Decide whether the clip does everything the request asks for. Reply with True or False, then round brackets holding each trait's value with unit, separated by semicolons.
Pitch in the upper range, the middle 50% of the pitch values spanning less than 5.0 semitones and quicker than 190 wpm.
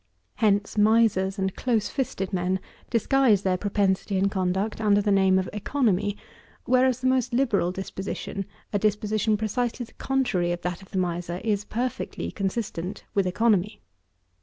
False (205 Hz; 3.1 semitones; 150 wpm)